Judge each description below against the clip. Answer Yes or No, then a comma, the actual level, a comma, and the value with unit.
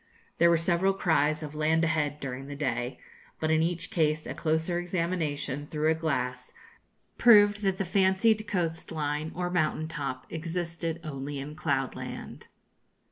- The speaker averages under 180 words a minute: Yes, average, 155 wpm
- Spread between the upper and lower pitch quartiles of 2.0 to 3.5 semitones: Yes, average, 3.0 semitones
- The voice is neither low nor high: Yes, medium, 160 Hz